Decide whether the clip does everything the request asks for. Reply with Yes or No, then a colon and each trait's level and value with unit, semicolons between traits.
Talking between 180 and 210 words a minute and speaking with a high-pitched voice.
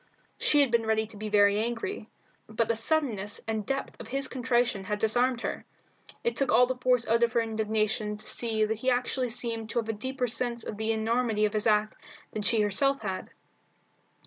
Yes: fast, 205 wpm; high, 225 Hz